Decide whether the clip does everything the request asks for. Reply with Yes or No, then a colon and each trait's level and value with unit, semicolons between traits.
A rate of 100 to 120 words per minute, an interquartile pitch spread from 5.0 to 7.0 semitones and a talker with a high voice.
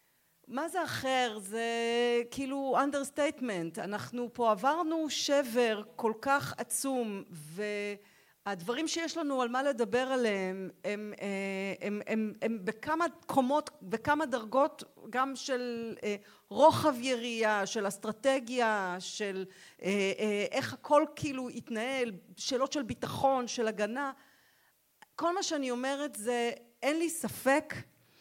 No: average, 115 wpm; average, 4.6 semitones; high, 240 Hz